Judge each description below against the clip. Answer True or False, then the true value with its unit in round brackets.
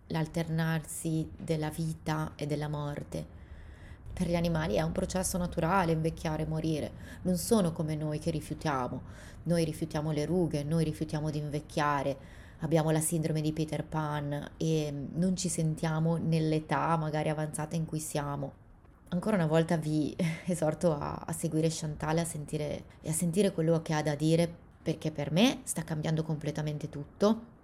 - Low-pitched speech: False (155 Hz)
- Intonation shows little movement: True (1.8 semitones)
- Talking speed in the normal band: True (150 wpm)